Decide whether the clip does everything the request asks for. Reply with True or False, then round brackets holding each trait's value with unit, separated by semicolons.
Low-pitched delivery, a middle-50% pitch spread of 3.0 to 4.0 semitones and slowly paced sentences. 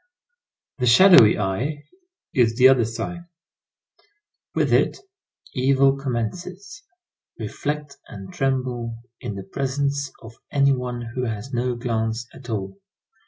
True (125 Hz; 3.4 semitones; 120 wpm)